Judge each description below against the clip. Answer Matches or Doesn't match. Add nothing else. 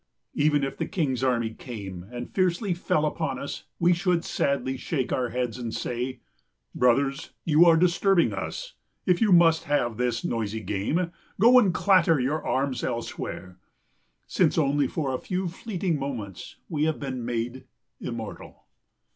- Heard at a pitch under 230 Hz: Matches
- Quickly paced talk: Doesn't match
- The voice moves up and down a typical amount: Doesn't match